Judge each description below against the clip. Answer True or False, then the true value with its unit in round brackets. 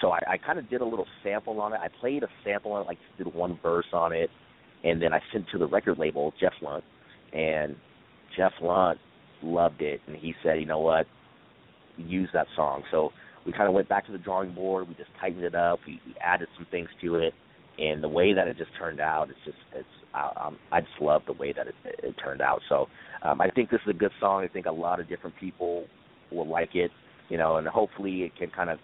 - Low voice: True (85 Hz)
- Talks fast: True (250 wpm)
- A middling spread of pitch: True (3.0 semitones)